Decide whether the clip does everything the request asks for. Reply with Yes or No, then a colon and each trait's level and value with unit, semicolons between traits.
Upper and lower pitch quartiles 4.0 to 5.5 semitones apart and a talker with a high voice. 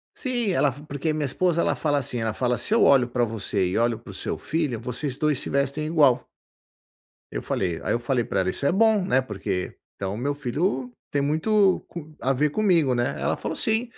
No: average, 5.2 semitones; medium, 140 Hz